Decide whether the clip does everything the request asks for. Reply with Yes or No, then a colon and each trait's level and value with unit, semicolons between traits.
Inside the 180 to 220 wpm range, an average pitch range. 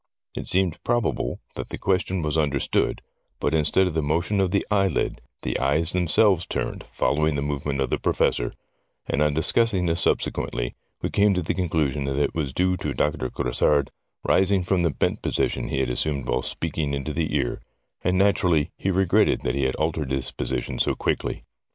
Yes: average, 190 wpm; average, 4.5 semitones